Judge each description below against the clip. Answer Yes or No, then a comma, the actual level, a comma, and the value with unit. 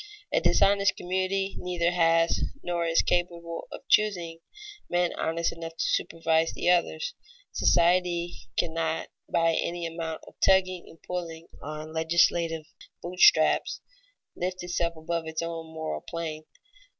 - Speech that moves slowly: Yes, slow, 130 wpm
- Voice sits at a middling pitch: Yes, medium, 170 Hz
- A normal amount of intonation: No, narrow, 1.4 semitones